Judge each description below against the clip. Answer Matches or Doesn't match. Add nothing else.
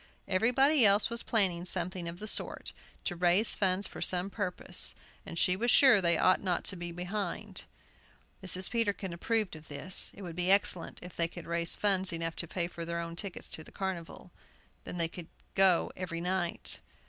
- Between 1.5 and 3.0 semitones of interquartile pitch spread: Matches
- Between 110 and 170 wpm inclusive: Doesn't match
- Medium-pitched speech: Matches